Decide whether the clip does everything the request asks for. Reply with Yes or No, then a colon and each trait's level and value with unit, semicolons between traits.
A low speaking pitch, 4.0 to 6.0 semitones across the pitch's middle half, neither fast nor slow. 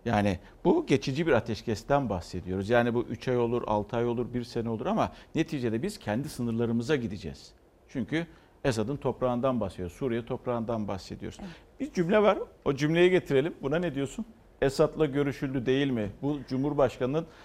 No: low, 125 Hz; average, 4.6 semitones; fast, 155 wpm